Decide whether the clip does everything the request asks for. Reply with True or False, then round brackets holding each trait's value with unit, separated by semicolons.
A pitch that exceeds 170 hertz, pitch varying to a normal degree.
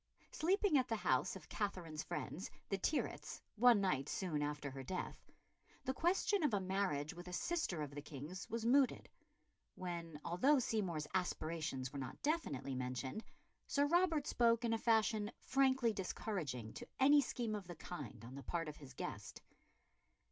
False (190 Hz; 8.7 semitones)